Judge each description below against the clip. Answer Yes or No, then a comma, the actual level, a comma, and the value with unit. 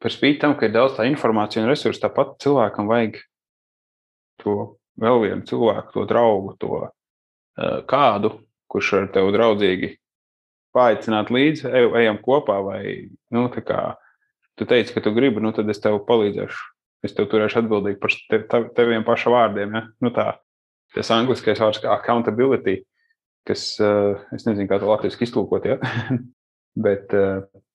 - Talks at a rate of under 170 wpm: Yes, average, 140 wpm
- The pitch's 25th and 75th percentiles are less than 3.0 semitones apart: Yes, narrow, 2.6 semitones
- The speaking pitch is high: No, low, 110 Hz